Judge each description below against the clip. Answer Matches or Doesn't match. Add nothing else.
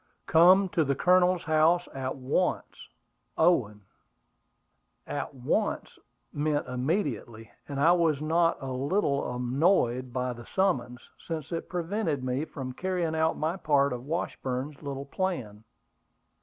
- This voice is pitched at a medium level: Matches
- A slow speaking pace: Matches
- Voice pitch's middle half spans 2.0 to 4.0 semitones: Doesn't match